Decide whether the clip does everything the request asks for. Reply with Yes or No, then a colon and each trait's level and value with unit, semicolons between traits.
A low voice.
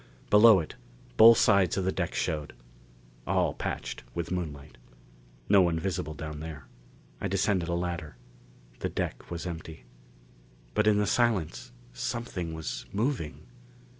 Yes: very low, 85 Hz